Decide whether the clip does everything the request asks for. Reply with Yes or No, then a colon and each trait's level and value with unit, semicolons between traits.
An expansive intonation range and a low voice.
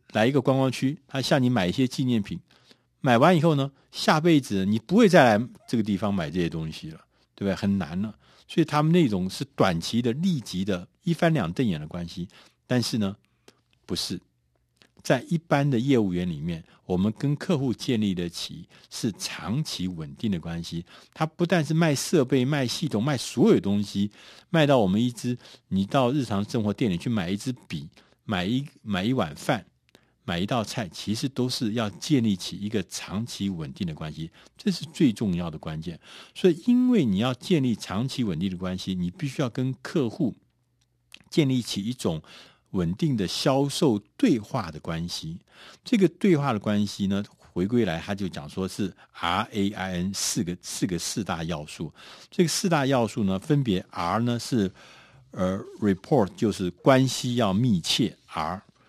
Yes: wide, 7.2 semitones; low, 120 Hz